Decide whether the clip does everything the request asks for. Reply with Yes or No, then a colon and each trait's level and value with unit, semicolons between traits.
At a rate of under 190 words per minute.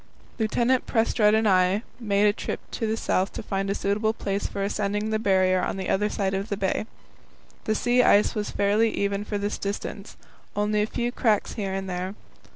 No: average, 200 wpm